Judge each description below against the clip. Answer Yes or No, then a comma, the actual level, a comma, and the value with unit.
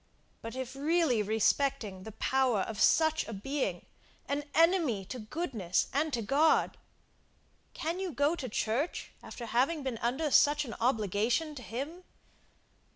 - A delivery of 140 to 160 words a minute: Yes, average, 145 wpm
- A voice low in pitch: No, very high, 265 Hz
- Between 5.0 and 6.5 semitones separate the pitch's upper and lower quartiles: Yes, average, 5.3 semitones